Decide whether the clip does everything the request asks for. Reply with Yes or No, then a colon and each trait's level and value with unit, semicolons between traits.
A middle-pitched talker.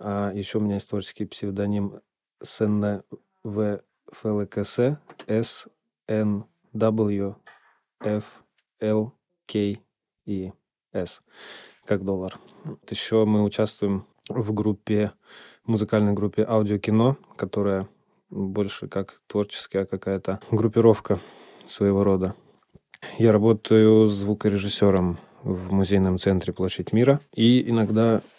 No: low, 105 Hz